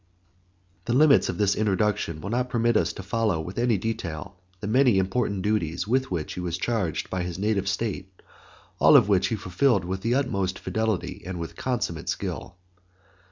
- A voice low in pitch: Yes, low, 100 Hz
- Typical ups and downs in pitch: Yes, average, 4.0 semitones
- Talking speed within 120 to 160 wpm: No, average, 180 wpm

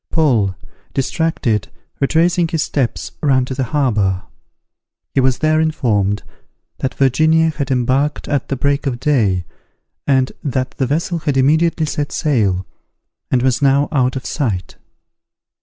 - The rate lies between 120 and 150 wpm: Yes, average, 140 wpm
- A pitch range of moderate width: Yes, average, 3.5 semitones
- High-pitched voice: No, low, 135 Hz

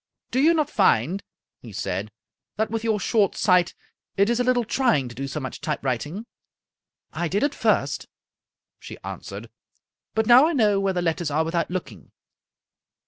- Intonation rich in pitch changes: Yes, wide, 7.5 semitones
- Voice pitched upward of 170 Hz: Yes, high, 190 Hz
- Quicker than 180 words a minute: Yes, average, 195 wpm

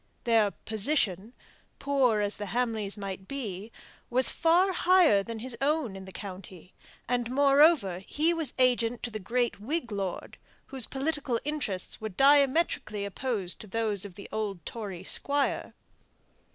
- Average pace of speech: Yes, average, 145 wpm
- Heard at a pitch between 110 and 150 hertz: No, high, 230 Hz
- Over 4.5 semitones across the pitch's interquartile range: Yes, wide, 5.6 semitones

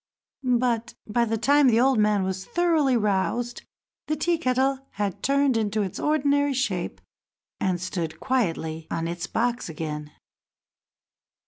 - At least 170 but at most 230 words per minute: No, slow, 135 wpm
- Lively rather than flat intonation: Yes, wide, 6.2 semitones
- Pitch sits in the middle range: No, high, 230 Hz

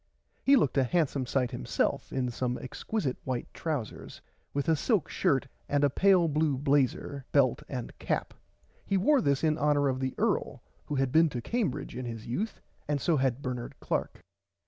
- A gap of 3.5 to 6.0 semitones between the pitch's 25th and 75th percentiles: Yes, average, 3.8 semitones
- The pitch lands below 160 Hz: Yes, medium, 140 Hz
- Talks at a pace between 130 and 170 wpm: No, average, 180 wpm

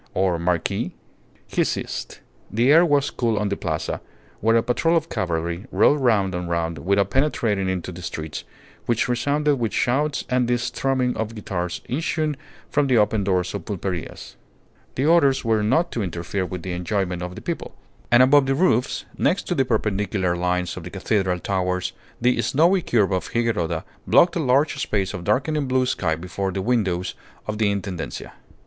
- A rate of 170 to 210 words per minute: Yes, average, 180 wpm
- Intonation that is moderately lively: No, wide, 6.2 semitones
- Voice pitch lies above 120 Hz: No, low, 105 Hz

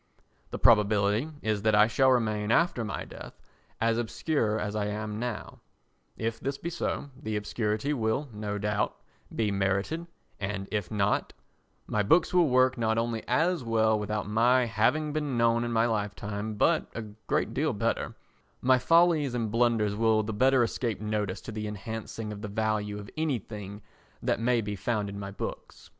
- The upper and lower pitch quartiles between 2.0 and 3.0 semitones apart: Yes, average, 2.7 semitones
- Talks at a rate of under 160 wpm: No, average, 175 wpm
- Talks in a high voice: No, low, 110 Hz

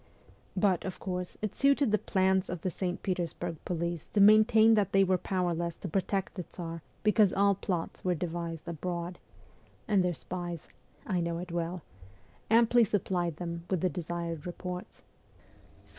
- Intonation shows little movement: Yes, narrow, 2.3 semitones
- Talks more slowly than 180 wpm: Yes, average, 160 wpm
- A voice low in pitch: No, medium, 180 Hz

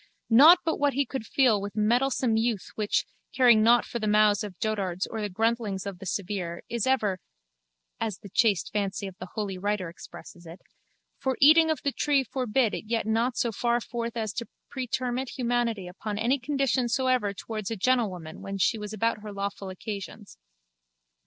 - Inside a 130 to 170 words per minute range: No, average, 185 wpm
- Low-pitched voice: No, high, 220 Hz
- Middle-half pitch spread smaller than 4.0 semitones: Yes, average, 3.6 semitones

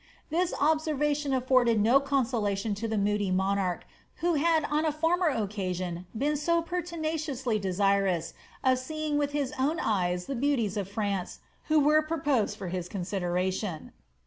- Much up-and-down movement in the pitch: Yes, wide, 7.3 semitones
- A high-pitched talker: Yes, very high, 250 Hz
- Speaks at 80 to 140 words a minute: No, average, 155 wpm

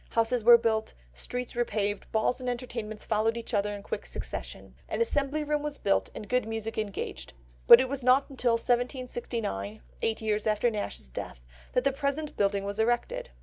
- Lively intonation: No, average, 3.0 semitones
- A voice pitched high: Yes, high, 230 Hz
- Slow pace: No, average, 180 wpm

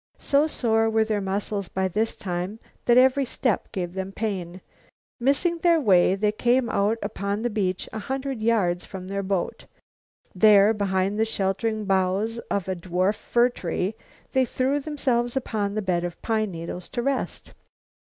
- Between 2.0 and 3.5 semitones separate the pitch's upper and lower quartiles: No, average, 4.0 semitones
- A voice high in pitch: Yes, high, 210 Hz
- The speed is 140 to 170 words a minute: Yes, average, 165 wpm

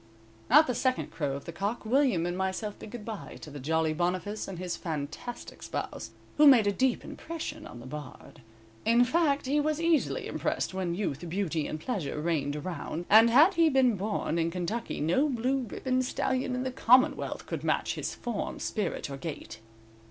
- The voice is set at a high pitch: Yes, high, 210 Hz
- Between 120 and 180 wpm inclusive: No, average, 190 wpm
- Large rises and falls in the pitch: Yes, wide, 7.5 semitones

